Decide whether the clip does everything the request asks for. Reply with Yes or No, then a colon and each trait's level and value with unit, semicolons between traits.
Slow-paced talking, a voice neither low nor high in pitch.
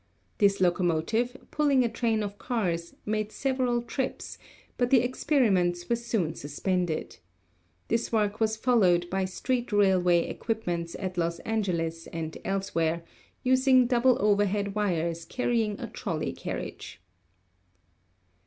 No: slow, 120 wpm; high, 205 Hz